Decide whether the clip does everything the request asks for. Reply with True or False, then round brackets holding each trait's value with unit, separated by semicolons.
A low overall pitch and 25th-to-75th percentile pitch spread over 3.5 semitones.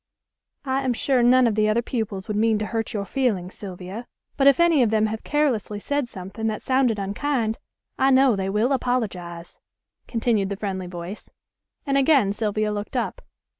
False (220 Hz; 4.3 semitones)